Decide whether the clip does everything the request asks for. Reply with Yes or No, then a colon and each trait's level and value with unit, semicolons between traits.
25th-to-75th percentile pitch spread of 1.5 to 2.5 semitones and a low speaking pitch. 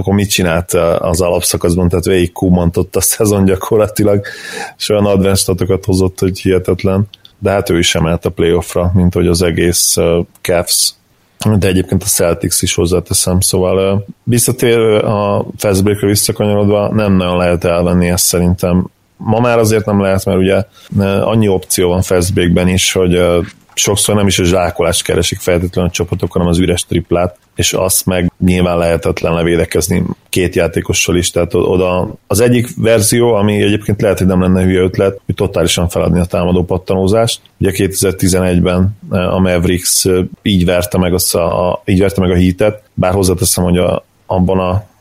Yes: narrow, 2.1 semitones; very low, 95 Hz